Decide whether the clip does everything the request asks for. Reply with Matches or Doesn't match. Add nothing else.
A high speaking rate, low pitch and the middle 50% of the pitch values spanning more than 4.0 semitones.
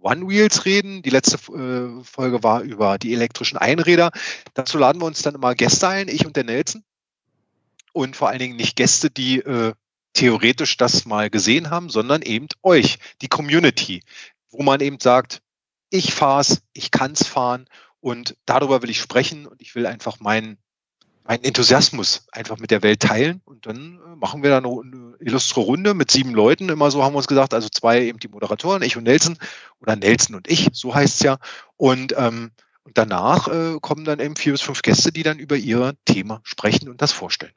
Matches